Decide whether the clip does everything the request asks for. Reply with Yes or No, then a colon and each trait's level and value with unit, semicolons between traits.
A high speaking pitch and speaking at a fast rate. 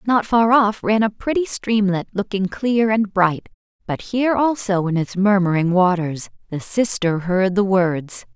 No: high, 200 Hz; average, 165 wpm